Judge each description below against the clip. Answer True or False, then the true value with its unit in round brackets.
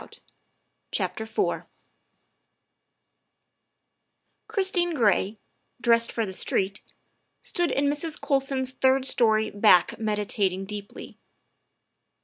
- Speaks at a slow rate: True (100 wpm)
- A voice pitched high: True (230 Hz)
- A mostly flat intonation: False (5.0 semitones)